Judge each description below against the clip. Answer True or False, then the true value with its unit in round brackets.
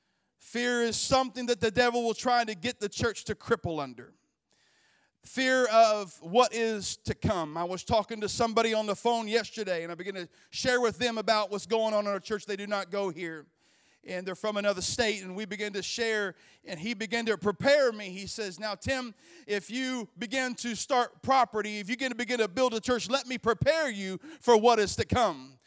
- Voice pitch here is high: True (225 Hz)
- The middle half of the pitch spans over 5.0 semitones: False (3.3 semitones)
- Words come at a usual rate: False (215 wpm)